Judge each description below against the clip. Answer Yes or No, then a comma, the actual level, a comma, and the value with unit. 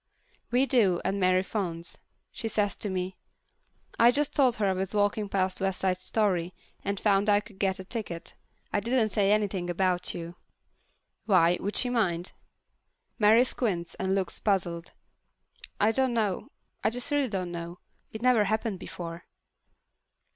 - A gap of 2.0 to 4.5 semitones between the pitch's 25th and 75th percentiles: Yes, average, 3.1 semitones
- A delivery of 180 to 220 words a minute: No, average, 160 wpm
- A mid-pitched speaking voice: No, high, 195 Hz